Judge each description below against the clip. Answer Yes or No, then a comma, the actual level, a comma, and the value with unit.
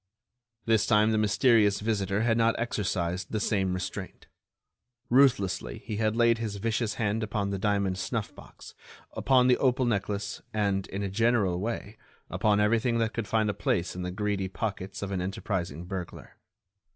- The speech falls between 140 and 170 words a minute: Yes, average, 165 wpm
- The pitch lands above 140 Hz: No, low, 105 Hz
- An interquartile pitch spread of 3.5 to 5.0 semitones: No, average, 2.7 semitones